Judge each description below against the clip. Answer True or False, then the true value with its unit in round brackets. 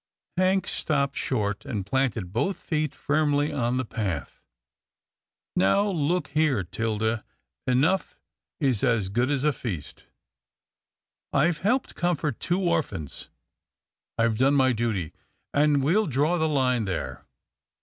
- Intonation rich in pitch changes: True (5.7 semitones)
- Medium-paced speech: False (130 wpm)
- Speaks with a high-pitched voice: False (135 Hz)